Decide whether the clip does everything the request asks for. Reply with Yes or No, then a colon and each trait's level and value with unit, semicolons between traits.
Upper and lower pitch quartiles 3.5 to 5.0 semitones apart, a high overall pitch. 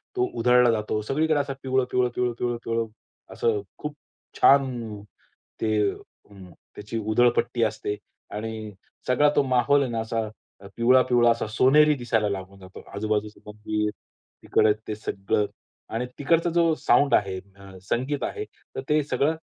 No: average, 4.0 semitones; low, 115 Hz